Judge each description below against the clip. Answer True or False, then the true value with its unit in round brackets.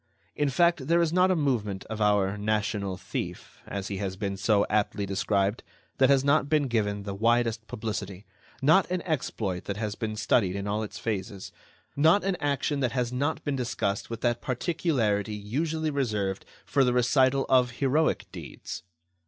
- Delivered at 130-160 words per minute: False (175 wpm)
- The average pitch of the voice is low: True (115 Hz)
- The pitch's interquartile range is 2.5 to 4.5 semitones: False (5.5 semitones)